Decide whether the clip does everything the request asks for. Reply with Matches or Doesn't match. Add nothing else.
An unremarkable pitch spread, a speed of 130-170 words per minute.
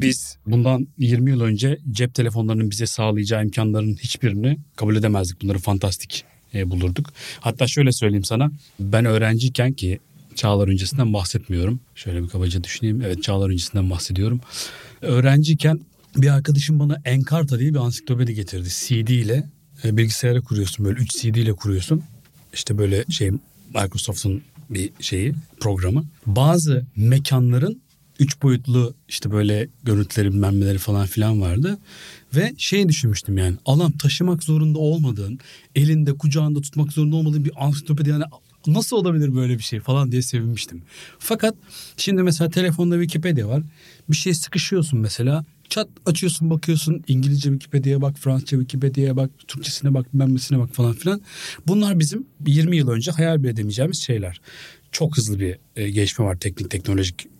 Doesn't match